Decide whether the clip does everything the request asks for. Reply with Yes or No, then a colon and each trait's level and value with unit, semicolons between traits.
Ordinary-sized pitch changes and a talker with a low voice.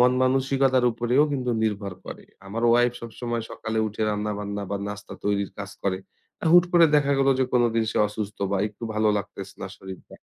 Yes: average, 3.7 semitones; low, 115 Hz